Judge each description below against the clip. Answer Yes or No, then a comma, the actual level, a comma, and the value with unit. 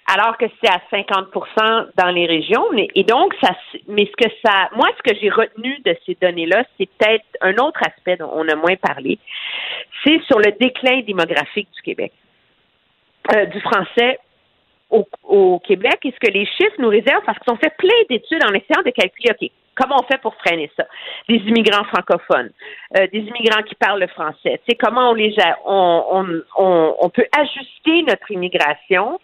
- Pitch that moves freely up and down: Yes, wide, 6.3 semitones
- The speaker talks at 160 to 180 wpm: No, average, 195 wpm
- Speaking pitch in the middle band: No, high, 225 Hz